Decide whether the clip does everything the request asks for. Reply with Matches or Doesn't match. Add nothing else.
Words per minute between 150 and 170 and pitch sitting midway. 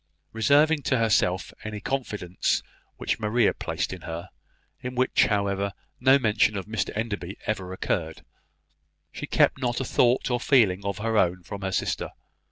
Doesn't match